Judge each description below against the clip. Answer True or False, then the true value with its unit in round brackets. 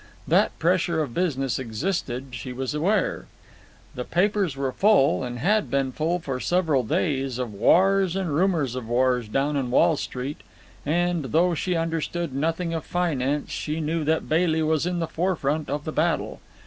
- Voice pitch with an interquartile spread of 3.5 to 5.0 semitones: True (4.6 semitones)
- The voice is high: False (155 Hz)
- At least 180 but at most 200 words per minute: False (170 wpm)